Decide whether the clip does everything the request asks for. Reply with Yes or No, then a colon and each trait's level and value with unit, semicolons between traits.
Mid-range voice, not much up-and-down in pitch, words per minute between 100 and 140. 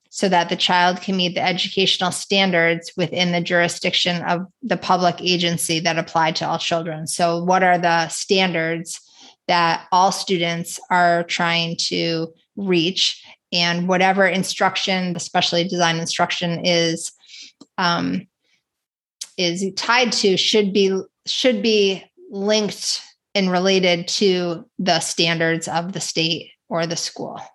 Yes: medium, 175 Hz; narrow, 2.0 semitones; slow, 135 wpm